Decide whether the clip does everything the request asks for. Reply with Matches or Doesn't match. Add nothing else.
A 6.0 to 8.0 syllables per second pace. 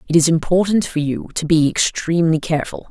Matches